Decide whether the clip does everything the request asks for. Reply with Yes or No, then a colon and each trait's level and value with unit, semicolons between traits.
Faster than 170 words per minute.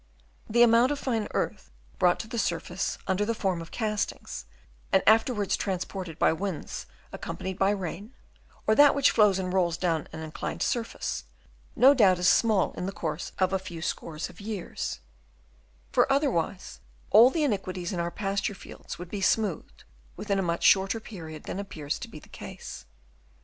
Yes: average, 180 wpm